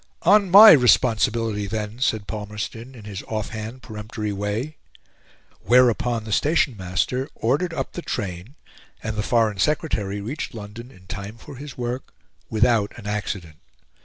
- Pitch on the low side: Yes, low, 110 Hz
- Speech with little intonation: No, average, 3.6 semitones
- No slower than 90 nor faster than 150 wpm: Yes, average, 145 wpm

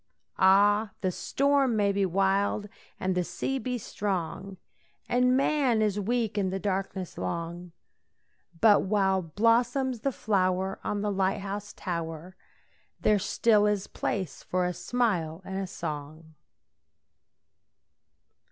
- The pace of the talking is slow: Yes, slow, 125 wpm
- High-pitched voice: Yes, high, 195 Hz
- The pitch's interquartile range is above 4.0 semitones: No, average, 2.8 semitones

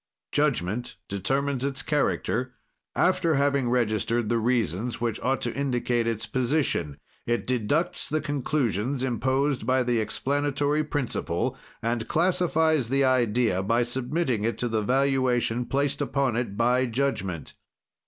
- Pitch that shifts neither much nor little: Yes, average, 3.2 semitones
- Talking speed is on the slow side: Yes, slow, 130 wpm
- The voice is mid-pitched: No, low, 125 Hz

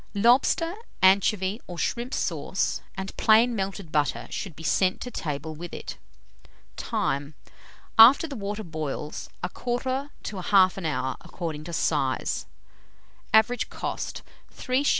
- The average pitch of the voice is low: No, high, 195 Hz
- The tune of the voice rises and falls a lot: Yes, wide, 6.7 semitones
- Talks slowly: Yes, slow, 125 wpm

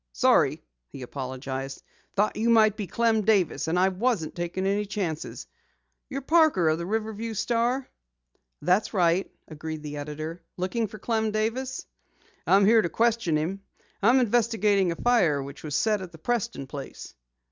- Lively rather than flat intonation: Yes, wide, 5.9 semitones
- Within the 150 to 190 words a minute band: Yes, average, 160 wpm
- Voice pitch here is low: No, high, 195 Hz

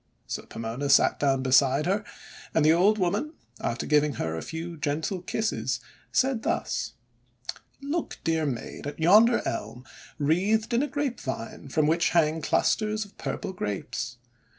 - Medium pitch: Yes, medium, 160 Hz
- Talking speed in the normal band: Yes, average, 150 wpm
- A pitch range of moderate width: No, wide, 7.0 semitones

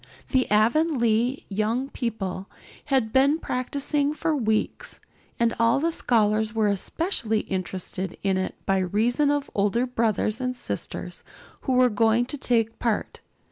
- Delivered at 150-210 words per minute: No, average, 140 wpm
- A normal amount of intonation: Yes, average, 3.7 semitones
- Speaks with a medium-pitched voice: No, high, 230 Hz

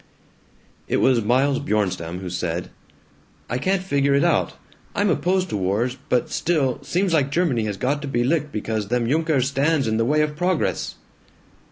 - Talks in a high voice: No, low, 135 Hz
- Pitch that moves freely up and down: Yes, wide, 5.9 semitones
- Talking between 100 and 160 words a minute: No, average, 175 wpm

